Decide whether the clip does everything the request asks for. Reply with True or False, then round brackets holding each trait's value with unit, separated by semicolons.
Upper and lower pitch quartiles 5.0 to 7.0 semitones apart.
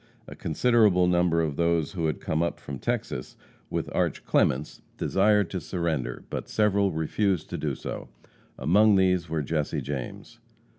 False (3.9 semitones)